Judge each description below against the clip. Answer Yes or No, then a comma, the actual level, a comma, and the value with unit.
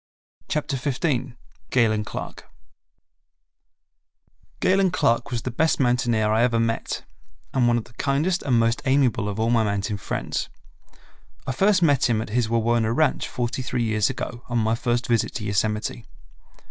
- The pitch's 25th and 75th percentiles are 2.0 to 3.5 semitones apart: Yes, average, 2.9 semitones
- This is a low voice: Yes, low, 120 Hz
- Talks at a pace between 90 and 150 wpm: No, average, 160 wpm